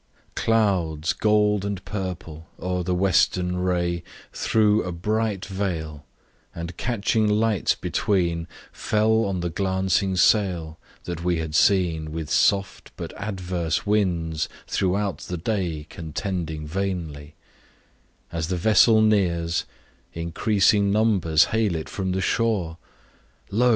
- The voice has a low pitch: Yes, very low, 90 Hz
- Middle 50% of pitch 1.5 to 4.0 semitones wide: Yes, average, 3.7 semitones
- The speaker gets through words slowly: Yes, slow, 120 wpm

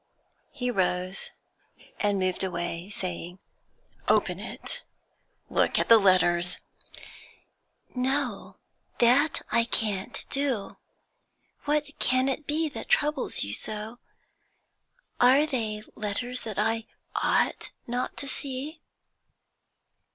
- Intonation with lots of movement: Yes, wide, 5.7 semitones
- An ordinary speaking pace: No, slow, 100 wpm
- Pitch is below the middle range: No, high, 230 Hz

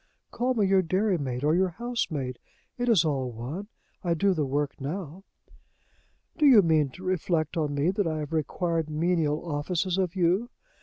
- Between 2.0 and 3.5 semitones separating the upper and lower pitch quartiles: No, average, 4.2 semitones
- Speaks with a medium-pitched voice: Yes, medium, 170 Hz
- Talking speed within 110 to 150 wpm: No, average, 170 wpm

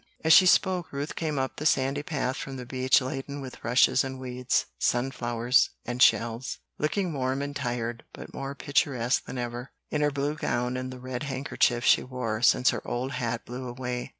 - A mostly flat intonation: Yes, narrow, 2.3 semitones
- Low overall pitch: Yes, low, 130 Hz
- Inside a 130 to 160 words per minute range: No, average, 195 wpm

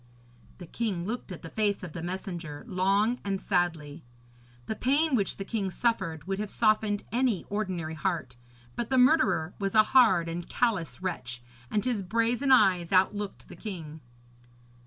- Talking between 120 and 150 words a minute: No, average, 165 wpm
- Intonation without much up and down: No, average, 4.5 semitones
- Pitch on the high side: Yes, high, 195 Hz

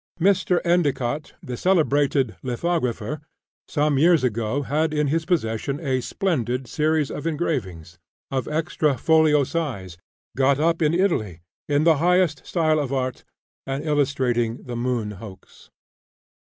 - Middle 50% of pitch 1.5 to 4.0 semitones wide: No, average, 4.4 semitones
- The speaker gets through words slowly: Yes, slow, 130 wpm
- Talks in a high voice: No, medium, 145 Hz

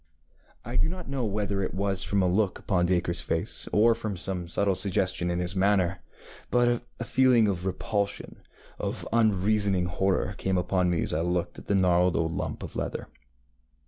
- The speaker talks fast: No, average, 185 wpm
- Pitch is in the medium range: No, very low, 95 Hz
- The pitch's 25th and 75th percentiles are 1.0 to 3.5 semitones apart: Yes, average, 2.8 semitones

